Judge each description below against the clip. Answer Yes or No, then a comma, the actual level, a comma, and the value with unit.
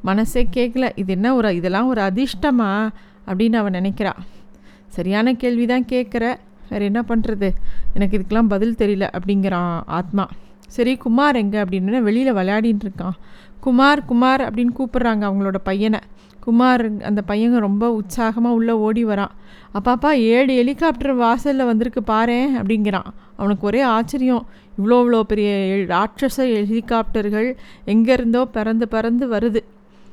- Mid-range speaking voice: No, high, 225 Hz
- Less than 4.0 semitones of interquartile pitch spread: Yes, average, 3.3 semitones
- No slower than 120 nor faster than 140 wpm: Yes, average, 125 wpm